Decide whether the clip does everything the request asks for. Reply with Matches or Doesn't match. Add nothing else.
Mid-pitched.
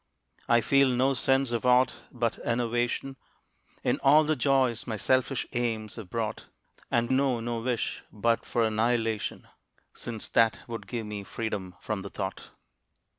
Doesn't match